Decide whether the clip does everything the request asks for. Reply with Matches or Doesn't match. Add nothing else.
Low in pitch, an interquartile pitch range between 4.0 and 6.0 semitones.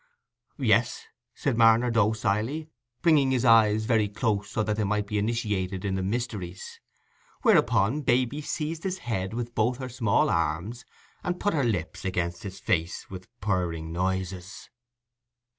Matches